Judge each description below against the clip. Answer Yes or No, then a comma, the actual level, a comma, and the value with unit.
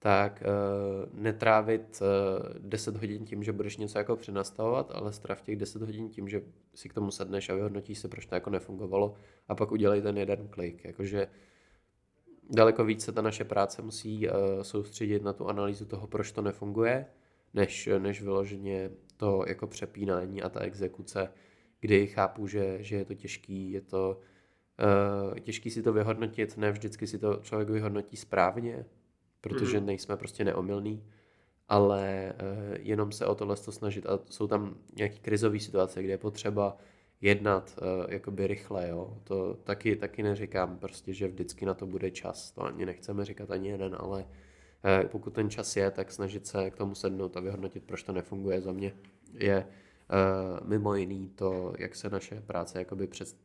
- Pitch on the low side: Yes, low, 100 Hz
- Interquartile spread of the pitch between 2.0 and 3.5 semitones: No, narrow, 1.6 semitones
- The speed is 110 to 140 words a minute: No, fast, 170 wpm